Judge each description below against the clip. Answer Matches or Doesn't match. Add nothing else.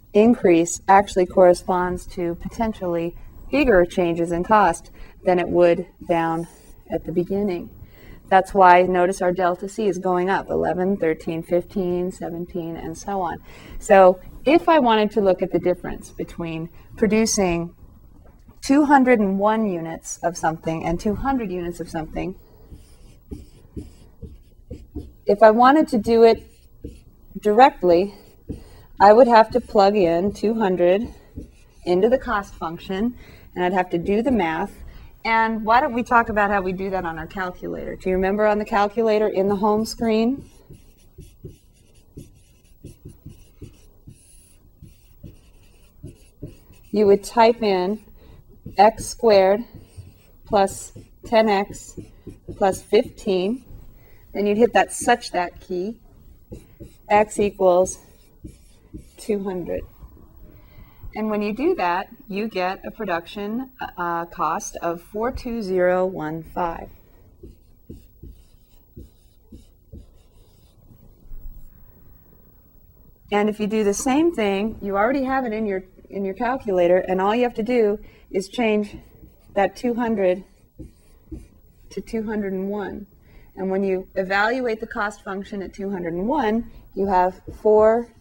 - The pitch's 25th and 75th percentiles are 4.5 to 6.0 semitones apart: Doesn't match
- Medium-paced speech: Doesn't match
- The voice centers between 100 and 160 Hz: Doesn't match